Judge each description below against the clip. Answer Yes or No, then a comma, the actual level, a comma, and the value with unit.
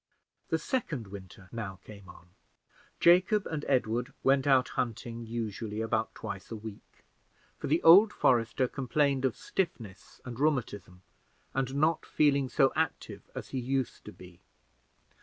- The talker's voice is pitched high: No, low, 125 Hz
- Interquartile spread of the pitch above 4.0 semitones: Yes, average, 4.6 semitones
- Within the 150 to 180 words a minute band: No, average, 140 wpm